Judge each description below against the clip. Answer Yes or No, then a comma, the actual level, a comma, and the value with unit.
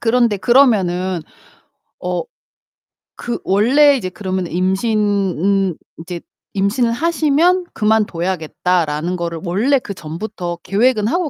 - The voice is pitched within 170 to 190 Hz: No, high, 200 Hz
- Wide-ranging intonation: No, average, 5.0 semitones